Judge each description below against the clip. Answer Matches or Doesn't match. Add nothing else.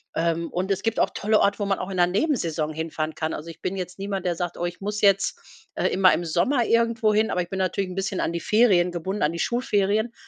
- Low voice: Doesn't match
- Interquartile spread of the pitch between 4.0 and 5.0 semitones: Doesn't match